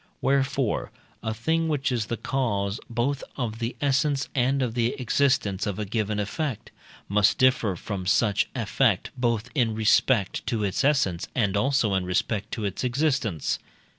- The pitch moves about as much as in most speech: Yes, average, 4.5 semitones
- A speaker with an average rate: Yes, average, 160 wpm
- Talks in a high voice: No, low, 115 Hz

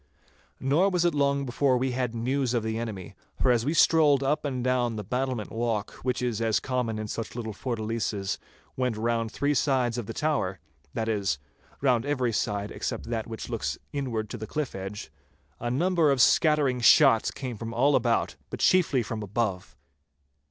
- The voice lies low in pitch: Yes, low, 120 Hz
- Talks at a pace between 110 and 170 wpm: No, average, 180 wpm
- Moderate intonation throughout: Yes, average, 3.6 semitones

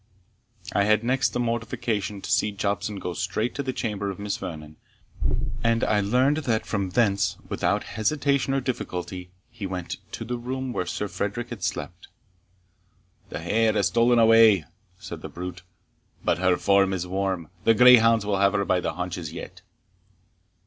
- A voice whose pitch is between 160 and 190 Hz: No, low, 105 Hz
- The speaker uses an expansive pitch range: No, average, 4.1 semitones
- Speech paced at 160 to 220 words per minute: Yes, average, 170 wpm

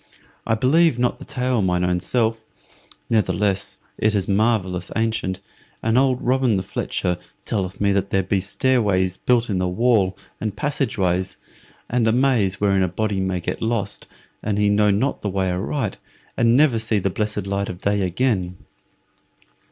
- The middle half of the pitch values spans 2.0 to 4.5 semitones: Yes, average, 3.7 semitones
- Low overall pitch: Yes, low, 105 Hz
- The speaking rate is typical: Yes, average, 170 wpm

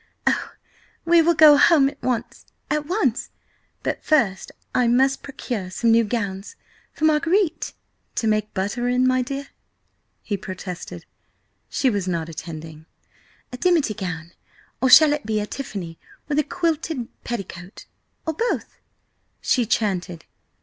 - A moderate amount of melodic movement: No, wide, 7.4 semitones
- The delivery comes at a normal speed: No, slow, 130 wpm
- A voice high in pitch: Yes, high, 240 Hz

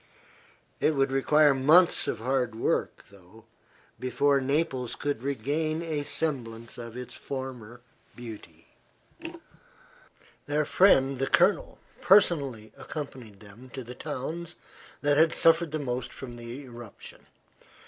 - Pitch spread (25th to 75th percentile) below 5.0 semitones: Yes, average, 3.9 semitones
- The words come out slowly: Yes, slow, 120 wpm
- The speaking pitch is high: No, low, 135 Hz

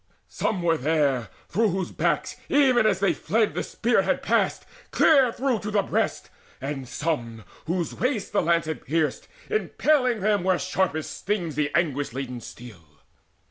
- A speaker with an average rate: Yes, average, 160 wpm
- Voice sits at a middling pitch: Yes, medium, 175 Hz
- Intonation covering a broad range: Yes, wide, 7.0 semitones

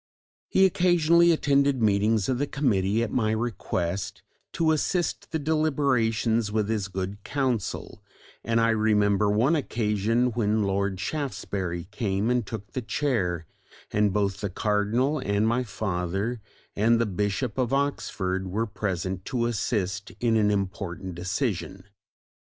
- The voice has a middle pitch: No, low, 110 Hz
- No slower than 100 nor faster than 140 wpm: Yes, slow, 135 wpm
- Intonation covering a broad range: No, average, 4.2 semitones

